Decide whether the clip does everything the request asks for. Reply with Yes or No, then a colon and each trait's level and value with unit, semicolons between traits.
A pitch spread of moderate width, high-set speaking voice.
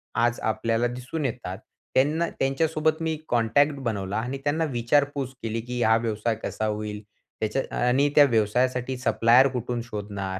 No: average, 3.7 semitones; low, 120 Hz